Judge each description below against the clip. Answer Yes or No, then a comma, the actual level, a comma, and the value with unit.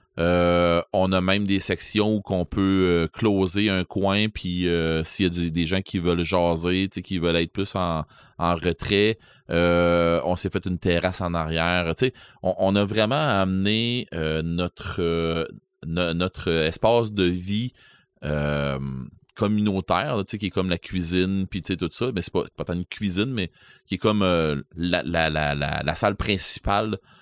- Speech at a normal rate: Yes, average, 180 wpm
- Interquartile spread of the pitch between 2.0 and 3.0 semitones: Yes, narrow, 2.5 semitones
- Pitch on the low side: Yes, very low, 90 Hz